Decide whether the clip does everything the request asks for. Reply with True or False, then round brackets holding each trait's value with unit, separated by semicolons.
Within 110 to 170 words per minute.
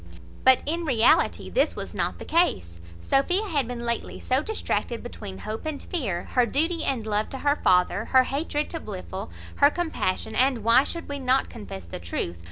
False (185 wpm)